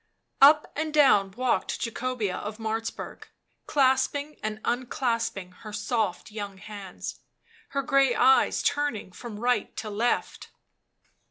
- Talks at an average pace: No, slow, 115 wpm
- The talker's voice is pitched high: Yes, high, 235 Hz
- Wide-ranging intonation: No, average, 4.1 semitones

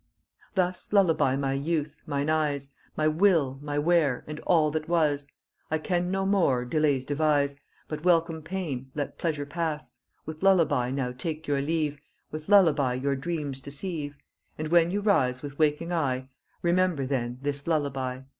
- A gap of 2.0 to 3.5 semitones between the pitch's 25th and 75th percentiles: Yes, average, 3.1 semitones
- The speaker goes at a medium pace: Yes, average, 155 wpm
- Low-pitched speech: No, medium, 150 Hz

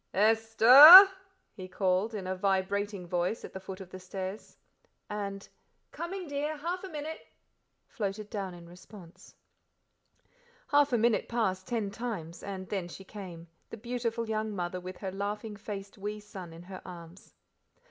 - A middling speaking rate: Yes, average, 155 wpm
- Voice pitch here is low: No, high, 200 Hz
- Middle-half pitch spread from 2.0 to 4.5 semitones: Yes, average, 3.4 semitones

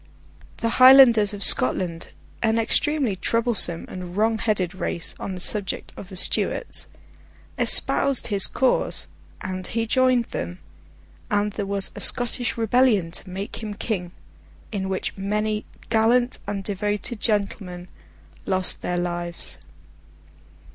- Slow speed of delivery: Yes, slow, 125 wpm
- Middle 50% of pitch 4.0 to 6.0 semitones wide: No, average, 3.6 semitones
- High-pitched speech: Yes, high, 205 Hz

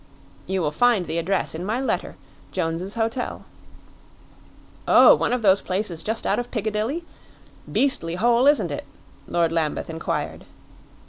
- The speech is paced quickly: No, average, 140 wpm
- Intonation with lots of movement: Yes, wide, 6.1 semitones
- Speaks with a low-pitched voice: No, high, 205 Hz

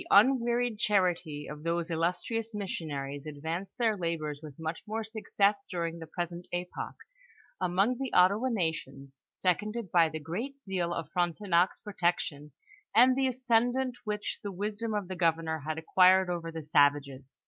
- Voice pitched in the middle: Yes, medium, 180 Hz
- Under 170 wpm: Yes, average, 160 wpm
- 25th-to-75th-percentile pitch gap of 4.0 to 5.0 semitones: Yes, average, 4.7 semitones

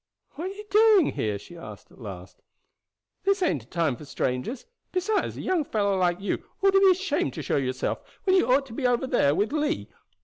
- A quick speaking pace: Yes, fast, 215 wpm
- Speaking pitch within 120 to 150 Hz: No, high, 245 Hz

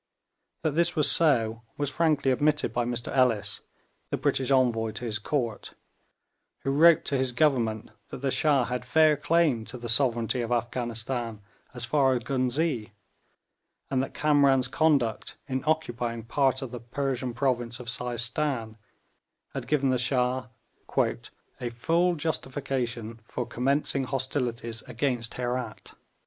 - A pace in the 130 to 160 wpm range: Yes, average, 140 wpm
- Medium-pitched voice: No, low, 125 Hz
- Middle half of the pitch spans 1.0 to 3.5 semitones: Yes, average, 3.1 semitones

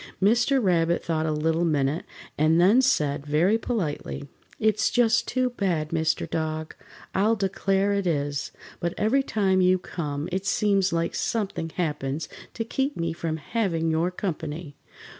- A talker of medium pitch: Yes, medium, 175 Hz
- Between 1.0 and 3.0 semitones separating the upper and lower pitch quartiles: No, average, 4.5 semitones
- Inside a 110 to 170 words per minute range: Yes, average, 150 wpm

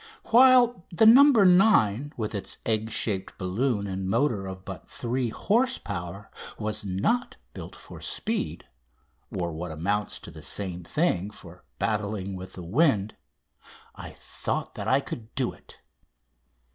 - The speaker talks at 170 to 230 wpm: No, average, 145 wpm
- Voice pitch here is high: No, low, 110 Hz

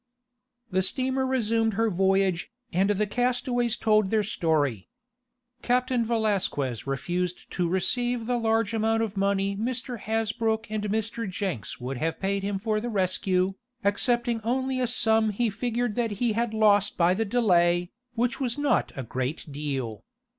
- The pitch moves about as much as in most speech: Yes, average, 4.0 semitones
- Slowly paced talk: No, average, 155 wpm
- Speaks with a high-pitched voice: Yes, high, 215 Hz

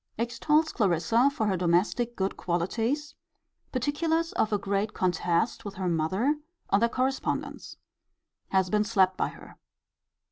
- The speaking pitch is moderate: No, high, 215 Hz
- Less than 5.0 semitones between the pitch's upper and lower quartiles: No, average, 5.3 semitones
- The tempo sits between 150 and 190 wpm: No, slow, 135 wpm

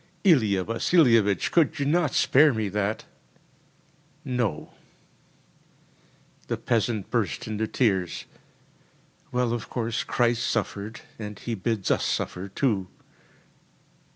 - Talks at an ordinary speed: No, slow, 105 wpm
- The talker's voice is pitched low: Yes, low, 115 Hz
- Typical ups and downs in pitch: Yes, average, 3.8 semitones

